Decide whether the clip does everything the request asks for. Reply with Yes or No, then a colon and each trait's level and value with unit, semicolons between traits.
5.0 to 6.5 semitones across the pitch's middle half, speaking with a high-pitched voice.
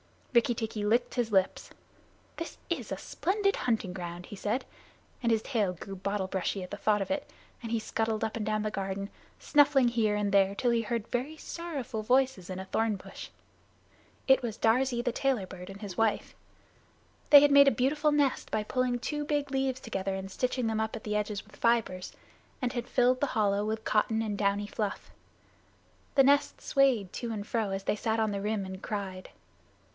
No: average, 4.1 semitones; high, 220 Hz